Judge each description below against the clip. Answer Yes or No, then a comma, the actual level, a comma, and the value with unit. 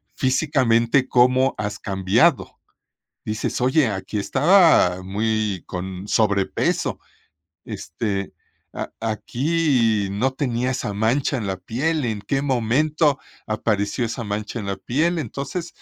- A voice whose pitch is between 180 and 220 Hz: No, low, 115 Hz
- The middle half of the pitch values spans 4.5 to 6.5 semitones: Yes, average, 4.8 semitones